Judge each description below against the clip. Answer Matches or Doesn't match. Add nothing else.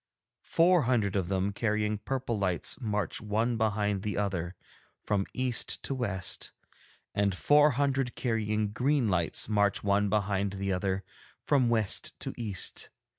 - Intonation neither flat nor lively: Matches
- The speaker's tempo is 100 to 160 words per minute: Matches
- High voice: Doesn't match